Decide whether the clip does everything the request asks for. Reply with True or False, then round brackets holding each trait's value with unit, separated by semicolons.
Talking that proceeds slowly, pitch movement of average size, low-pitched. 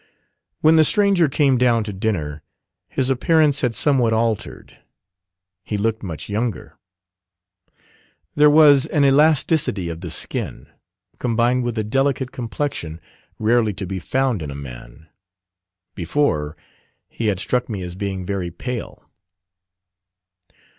False (125 wpm; 6.2 semitones; 115 Hz)